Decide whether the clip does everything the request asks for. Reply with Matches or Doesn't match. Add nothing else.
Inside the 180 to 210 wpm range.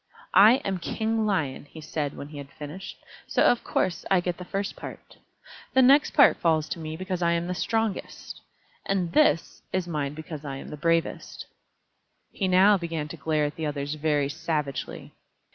Matches